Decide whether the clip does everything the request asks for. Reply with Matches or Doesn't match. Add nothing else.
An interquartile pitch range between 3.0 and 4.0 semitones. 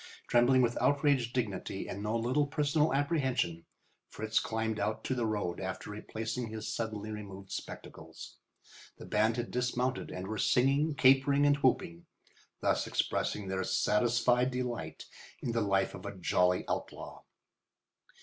Matches